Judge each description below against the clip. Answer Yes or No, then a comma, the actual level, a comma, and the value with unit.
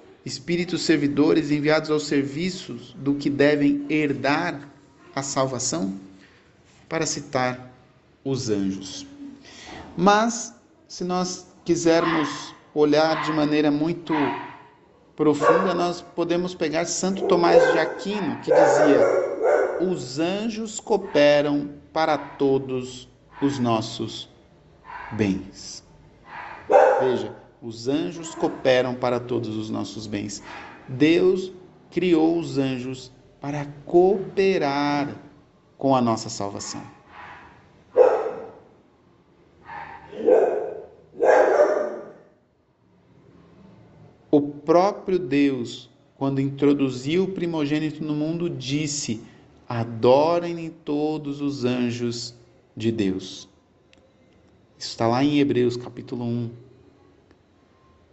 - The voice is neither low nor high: Yes, medium, 145 Hz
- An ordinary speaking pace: No, slow, 85 wpm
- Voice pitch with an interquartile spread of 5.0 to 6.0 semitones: Yes, average, 5.3 semitones